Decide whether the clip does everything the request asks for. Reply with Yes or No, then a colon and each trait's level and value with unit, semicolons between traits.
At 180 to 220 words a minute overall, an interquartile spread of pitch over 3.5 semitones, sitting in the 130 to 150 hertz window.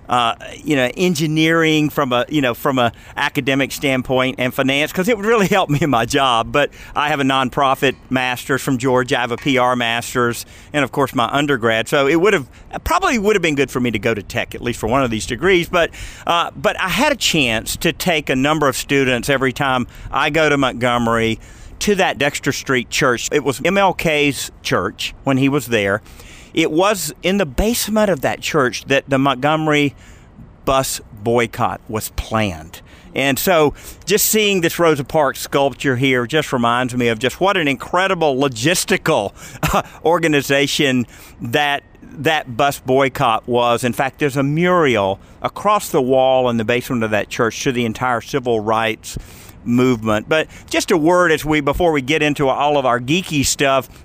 Yes: average, 190 wpm; average, 4.4 semitones; low, 135 Hz